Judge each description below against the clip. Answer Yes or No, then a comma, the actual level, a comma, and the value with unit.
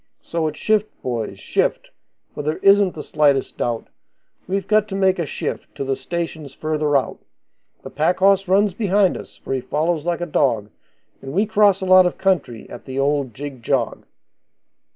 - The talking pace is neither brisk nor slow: Yes, average, 185 wpm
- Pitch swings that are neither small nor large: No, wide, 5.8 semitones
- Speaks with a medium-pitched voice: Yes, medium, 160 Hz